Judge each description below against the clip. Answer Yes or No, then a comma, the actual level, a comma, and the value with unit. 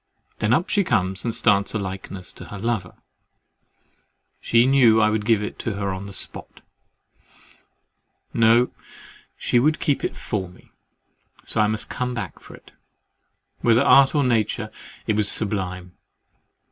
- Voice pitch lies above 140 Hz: No, low, 110 Hz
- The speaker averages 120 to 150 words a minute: Yes, average, 145 wpm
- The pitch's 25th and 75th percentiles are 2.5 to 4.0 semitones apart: Yes, average, 3.3 semitones